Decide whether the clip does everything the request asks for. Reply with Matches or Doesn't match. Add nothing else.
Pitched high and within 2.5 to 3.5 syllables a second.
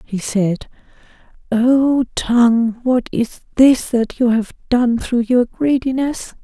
Matches